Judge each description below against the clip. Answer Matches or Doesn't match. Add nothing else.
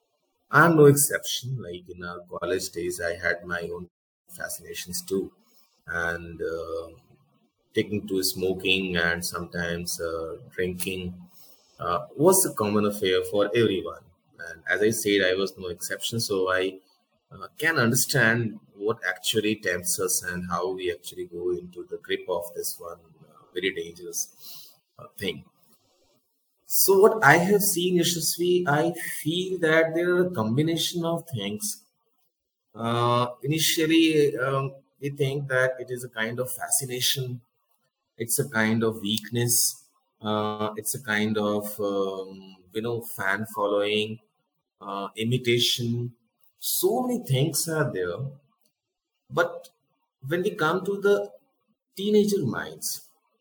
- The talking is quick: Doesn't match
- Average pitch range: Doesn't match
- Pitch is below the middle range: Matches